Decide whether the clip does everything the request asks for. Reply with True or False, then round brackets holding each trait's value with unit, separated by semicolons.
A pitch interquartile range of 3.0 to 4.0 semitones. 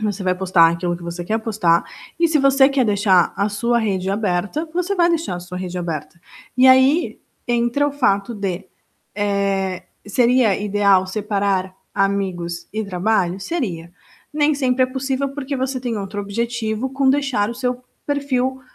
False (5.6 semitones)